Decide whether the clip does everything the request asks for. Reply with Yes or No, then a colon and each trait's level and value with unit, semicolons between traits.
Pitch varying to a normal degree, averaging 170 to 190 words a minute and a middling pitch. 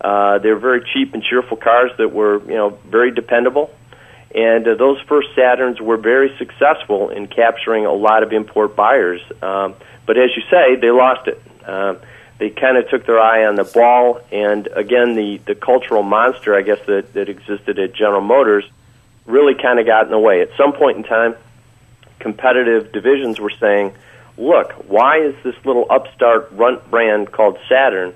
No: average, 3.1 semitones; average, 185 wpm; low, 115 Hz